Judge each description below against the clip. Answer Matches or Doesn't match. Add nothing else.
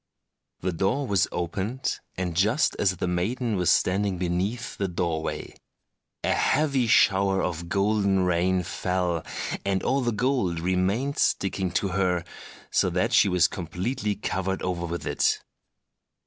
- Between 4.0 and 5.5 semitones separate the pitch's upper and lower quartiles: Doesn't match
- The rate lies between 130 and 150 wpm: Matches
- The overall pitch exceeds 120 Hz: Doesn't match